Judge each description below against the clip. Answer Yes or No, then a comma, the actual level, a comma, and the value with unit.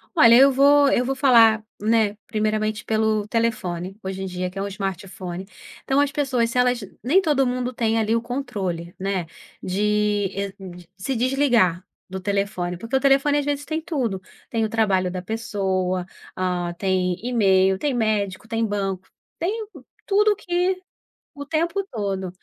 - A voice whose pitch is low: No, high, 220 Hz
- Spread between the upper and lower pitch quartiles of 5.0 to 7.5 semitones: Yes, wide, 5.6 semitones